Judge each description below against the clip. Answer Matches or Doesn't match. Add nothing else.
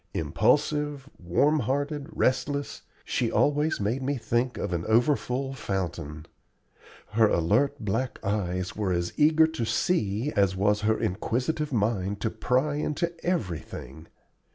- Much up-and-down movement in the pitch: Matches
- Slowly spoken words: Matches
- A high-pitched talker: Doesn't match